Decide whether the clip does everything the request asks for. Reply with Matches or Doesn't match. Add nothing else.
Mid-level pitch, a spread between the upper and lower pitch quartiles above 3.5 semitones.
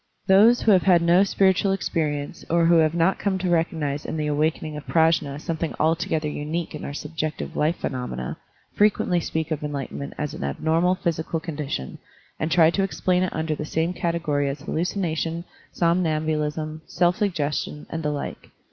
Doesn't match